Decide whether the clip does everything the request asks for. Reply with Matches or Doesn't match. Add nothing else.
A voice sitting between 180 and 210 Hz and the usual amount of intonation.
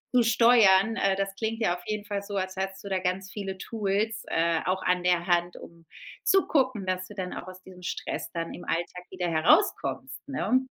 Matches